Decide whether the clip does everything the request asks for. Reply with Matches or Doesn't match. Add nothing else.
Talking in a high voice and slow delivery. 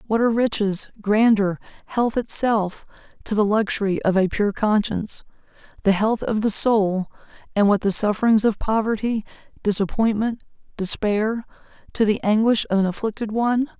Matches